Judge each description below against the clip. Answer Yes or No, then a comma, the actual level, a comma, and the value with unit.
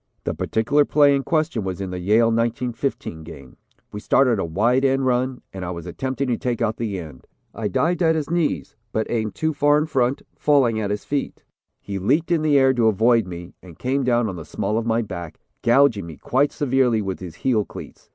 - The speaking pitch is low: Yes, low, 115 Hz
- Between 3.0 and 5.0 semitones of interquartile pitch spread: No, wide, 5.5 semitones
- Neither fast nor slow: No, fast, 220 wpm